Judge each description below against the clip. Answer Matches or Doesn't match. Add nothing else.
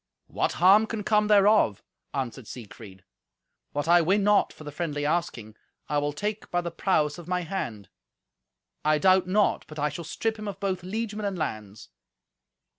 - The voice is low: Doesn't match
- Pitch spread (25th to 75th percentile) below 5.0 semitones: Doesn't match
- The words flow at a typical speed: Matches